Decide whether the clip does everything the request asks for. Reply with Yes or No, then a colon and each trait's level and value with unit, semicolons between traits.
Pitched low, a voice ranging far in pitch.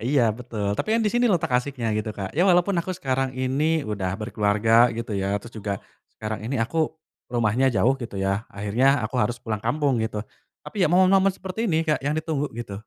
Yes: low, 125 Hz; wide, 6.5 semitones